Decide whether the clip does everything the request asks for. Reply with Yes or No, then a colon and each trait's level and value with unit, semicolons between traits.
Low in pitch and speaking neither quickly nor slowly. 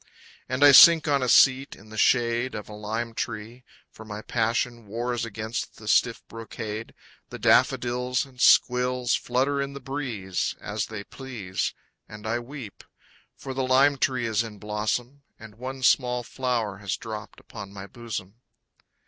Yes: low, 120 Hz; average, 160 wpm